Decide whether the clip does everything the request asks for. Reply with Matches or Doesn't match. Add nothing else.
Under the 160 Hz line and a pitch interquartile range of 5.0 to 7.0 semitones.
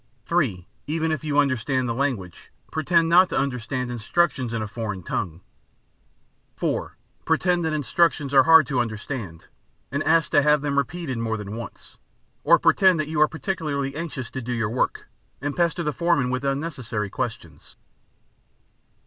Matches